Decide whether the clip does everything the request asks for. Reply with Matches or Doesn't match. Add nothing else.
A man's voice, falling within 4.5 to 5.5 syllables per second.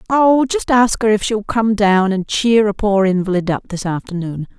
Doesn't match